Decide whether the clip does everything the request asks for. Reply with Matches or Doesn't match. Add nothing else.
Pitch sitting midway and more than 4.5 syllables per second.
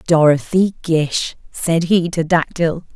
Doesn't match